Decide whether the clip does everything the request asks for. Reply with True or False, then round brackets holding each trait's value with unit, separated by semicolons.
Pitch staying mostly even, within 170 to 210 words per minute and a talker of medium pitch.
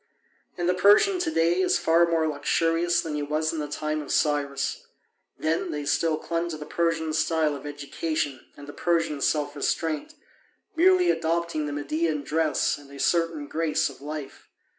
True (2.3 semitones; 175 wpm; 155 Hz)